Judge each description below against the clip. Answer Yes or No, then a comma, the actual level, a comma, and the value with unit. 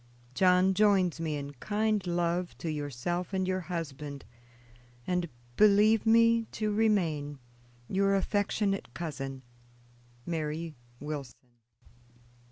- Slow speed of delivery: Yes, slow, 100 wpm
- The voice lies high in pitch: No, medium, 175 Hz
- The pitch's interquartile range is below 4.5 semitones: No, average, 5.2 semitones